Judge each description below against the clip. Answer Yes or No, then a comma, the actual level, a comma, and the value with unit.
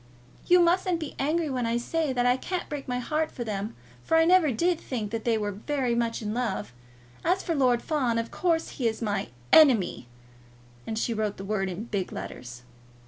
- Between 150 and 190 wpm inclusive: No, fast, 205 wpm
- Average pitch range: No, wide, 6.4 semitones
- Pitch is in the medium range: No, high, 245 Hz